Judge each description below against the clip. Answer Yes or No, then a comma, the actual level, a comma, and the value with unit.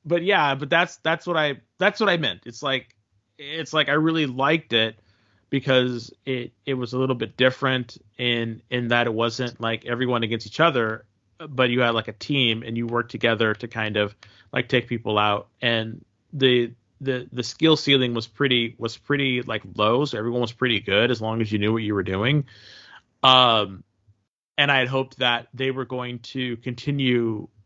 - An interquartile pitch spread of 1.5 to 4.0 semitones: Yes, average, 3.0 semitones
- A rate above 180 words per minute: Yes, average, 195 wpm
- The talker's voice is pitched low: Yes, low, 120 Hz